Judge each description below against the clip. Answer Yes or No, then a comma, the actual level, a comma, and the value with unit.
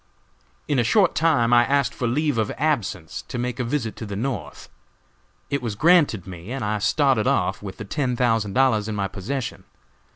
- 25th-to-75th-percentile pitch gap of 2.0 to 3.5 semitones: No, average, 4.7 semitones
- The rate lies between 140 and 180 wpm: No, average, 195 wpm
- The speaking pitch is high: No, low, 120 Hz